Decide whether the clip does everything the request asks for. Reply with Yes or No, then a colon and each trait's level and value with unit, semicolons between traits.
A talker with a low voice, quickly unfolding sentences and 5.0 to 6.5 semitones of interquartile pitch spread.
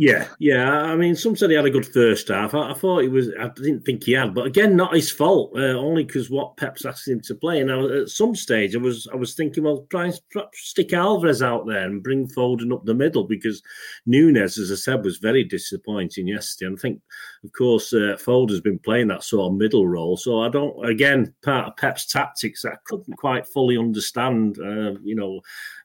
Yes: low, 125 Hz; fast, 230 wpm; wide, 5.5 semitones